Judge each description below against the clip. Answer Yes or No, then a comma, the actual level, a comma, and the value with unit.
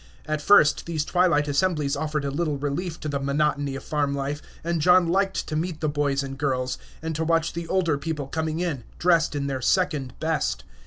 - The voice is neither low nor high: Yes, medium, 150 Hz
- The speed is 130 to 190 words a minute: No, fast, 205 wpm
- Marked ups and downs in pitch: No, average, 3.0 semitones